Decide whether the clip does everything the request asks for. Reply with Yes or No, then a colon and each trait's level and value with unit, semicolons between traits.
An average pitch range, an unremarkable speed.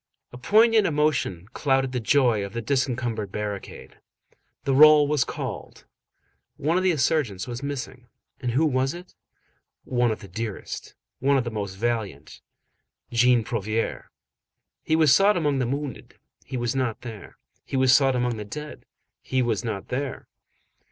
Yes: average, 4.1 semitones; average, 160 wpm